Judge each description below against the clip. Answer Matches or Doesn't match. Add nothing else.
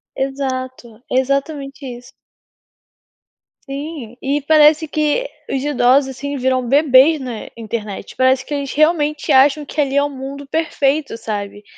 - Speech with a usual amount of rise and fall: Doesn't match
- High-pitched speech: Matches